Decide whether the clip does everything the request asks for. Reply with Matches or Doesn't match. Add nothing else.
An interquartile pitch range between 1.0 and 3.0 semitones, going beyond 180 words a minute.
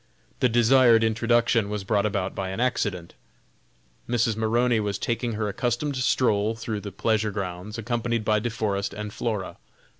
Doesn't match